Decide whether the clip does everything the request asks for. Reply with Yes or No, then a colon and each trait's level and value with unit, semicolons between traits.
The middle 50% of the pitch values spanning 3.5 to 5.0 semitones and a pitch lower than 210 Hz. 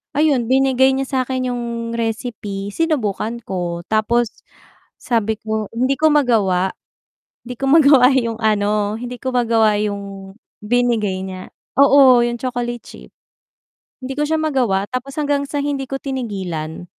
No: average, 4.2 semitones; high, 240 Hz